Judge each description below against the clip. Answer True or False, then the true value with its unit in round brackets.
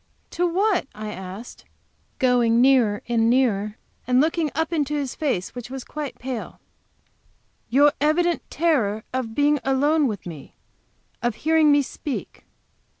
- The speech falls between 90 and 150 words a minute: True (145 wpm)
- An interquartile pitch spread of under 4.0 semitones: False (4.9 semitones)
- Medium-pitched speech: False (265 Hz)